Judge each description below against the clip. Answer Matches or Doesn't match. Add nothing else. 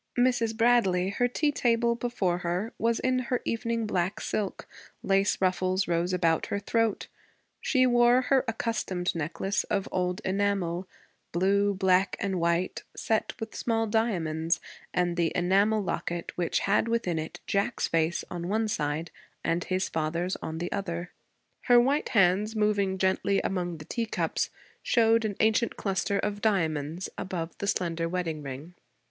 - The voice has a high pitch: Matches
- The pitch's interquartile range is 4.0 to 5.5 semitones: Matches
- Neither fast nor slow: Matches